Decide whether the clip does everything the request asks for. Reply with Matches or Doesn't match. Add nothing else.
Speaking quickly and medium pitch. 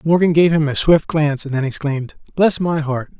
Matches